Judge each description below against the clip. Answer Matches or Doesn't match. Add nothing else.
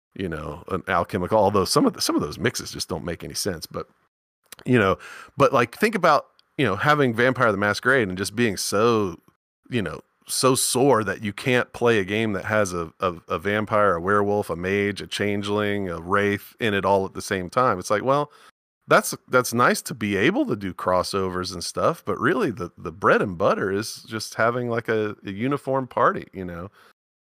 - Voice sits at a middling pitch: Doesn't match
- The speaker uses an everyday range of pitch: Matches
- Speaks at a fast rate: Matches